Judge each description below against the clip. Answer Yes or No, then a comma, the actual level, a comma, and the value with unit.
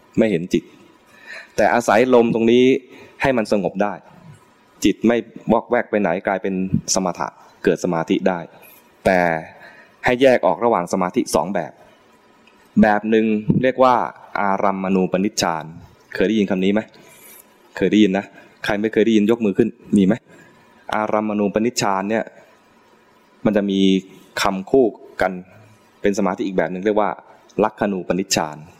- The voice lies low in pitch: Yes, low, 105 Hz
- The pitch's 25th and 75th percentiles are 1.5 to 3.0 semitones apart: Yes, narrow, 2.6 semitones